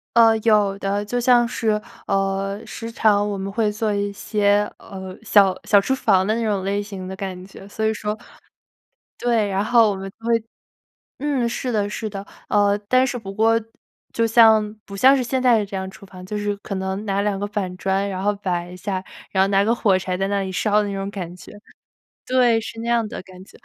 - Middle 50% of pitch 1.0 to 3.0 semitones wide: Yes, narrow, 2.4 semitones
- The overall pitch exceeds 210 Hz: No, high, 205 Hz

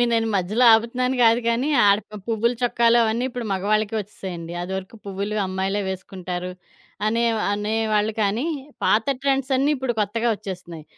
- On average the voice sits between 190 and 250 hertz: Yes, high, 215 Hz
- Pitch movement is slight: No, average, 3.4 semitones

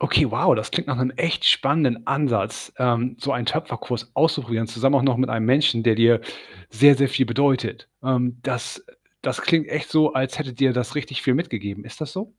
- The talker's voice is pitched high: No, low, 130 Hz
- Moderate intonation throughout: Yes, average, 3.4 semitones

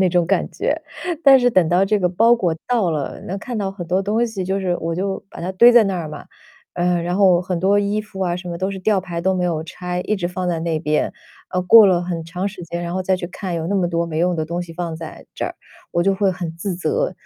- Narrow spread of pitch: Yes, narrow, 2.3 semitones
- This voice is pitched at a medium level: Yes, medium, 180 Hz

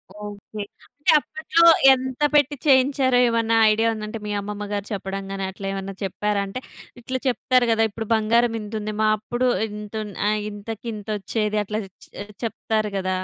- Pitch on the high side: Yes, high, 215 Hz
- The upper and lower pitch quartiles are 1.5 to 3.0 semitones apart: Yes, narrow, 2.5 semitones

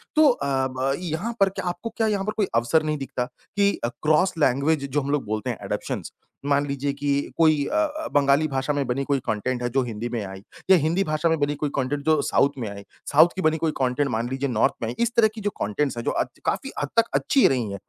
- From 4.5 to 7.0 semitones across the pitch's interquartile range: No, average, 4.0 semitones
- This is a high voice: No, medium, 145 Hz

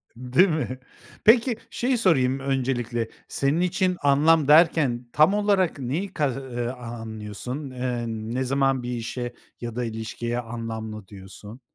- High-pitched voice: No, low, 130 Hz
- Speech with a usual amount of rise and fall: Yes, average, 4.6 semitones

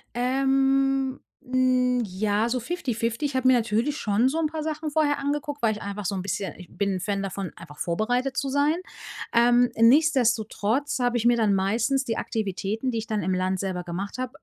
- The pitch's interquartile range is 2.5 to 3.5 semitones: No, average, 4.9 semitones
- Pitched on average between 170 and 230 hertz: No, high, 240 Hz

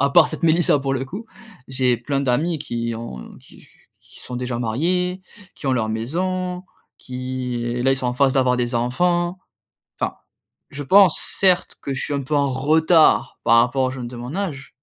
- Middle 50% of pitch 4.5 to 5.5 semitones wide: Yes, average, 4.9 semitones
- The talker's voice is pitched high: No, low, 135 Hz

